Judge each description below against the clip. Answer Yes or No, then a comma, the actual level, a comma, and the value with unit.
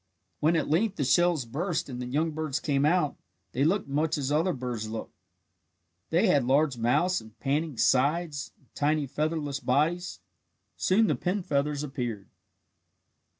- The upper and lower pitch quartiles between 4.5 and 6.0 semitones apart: No, average, 3.8 semitones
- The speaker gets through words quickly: No, average, 155 wpm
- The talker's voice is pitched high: No, medium, 150 Hz